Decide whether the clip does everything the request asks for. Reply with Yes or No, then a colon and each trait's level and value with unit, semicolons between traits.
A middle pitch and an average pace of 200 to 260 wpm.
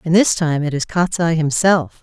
Yes: medium, 160 Hz; fast, 205 wpm